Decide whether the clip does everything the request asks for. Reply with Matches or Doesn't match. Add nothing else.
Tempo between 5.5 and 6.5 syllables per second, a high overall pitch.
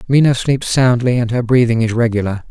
Doesn't match